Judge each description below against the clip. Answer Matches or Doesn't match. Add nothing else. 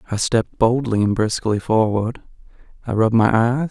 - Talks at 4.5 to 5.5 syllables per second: Matches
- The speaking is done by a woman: Doesn't match